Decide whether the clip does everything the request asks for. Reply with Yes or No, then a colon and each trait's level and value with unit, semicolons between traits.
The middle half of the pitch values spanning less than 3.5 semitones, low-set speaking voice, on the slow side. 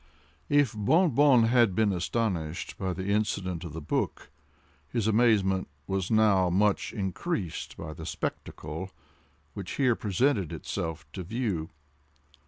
No: average, 4.3 semitones; low, 100 Hz; slow, 130 wpm